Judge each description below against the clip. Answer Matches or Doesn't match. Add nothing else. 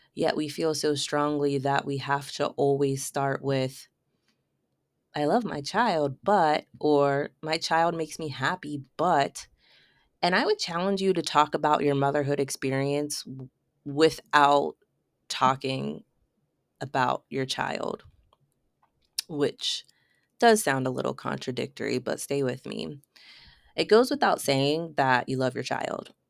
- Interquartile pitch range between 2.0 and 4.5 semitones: Matches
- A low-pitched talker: Doesn't match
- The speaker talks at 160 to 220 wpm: Doesn't match